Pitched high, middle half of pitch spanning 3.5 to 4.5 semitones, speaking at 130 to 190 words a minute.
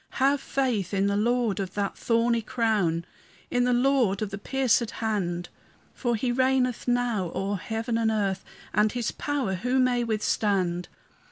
Yes: high, 225 Hz; average, 3.8 semitones; average, 160 wpm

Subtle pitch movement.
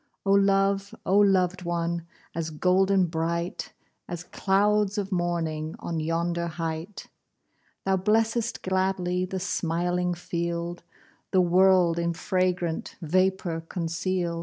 Yes: narrow, 2.1 semitones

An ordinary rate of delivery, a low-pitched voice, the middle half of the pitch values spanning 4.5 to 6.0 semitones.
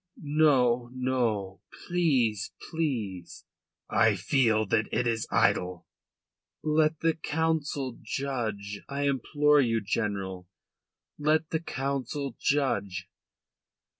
No: slow, 95 wpm; low, 125 Hz; wide, 5.6 semitones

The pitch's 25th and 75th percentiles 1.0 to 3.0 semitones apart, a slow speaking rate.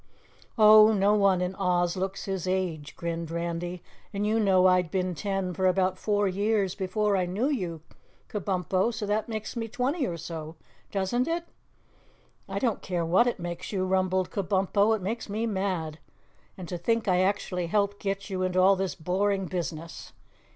No: narrow, 2.4 semitones; average, 175 wpm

